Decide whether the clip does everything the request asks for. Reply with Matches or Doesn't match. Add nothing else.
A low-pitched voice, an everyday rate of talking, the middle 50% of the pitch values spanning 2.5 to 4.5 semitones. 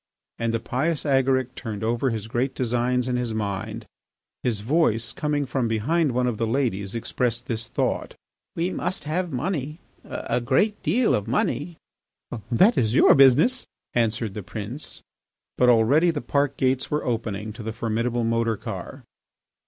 Matches